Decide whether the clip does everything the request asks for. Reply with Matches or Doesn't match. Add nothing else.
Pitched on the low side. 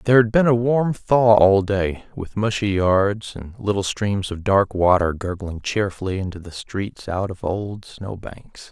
Matches